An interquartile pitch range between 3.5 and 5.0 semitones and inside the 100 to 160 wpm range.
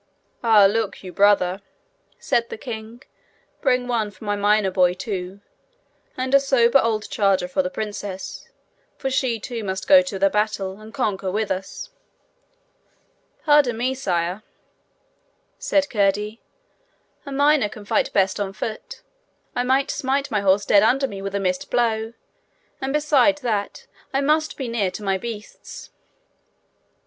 Yes: average, 4.5 semitones; average, 150 wpm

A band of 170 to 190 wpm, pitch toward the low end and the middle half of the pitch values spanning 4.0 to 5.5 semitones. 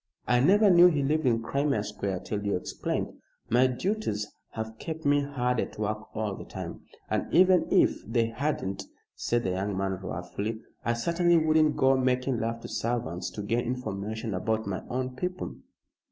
Yes: average, 175 wpm; low, 120 Hz; average, 5.2 semitones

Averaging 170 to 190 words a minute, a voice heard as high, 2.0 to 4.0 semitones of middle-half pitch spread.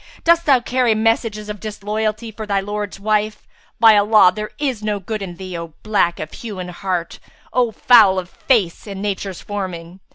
Yes: average, 185 wpm; high, 210 Hz; narrow, 2.6 semitones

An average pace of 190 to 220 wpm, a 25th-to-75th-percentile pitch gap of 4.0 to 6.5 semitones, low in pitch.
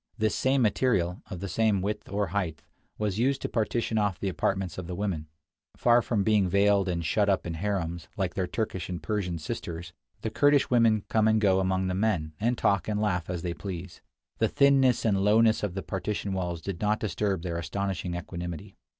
No: average, 200 wpm; average, 3.3 semitones; low, 100 Hz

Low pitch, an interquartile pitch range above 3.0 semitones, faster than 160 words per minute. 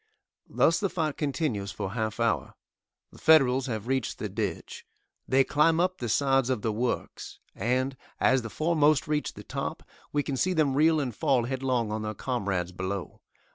Yes: low, 130 Hz; average, 5.3 semitones; average, 175 wpm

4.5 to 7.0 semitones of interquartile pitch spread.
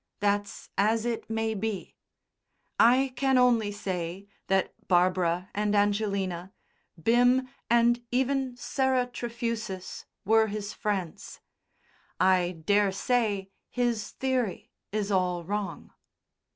No: average, 3.8 semitones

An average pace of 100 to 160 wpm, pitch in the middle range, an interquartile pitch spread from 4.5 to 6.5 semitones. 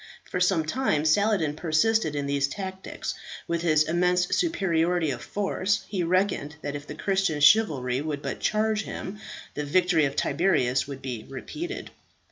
Yes: average, 155 wpm; medium, 170 Hz; average, 4.9 semitones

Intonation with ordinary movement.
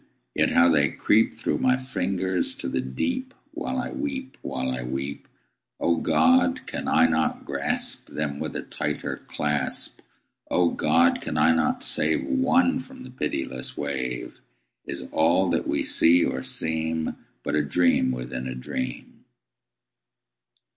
No: wide, 8.2 semitones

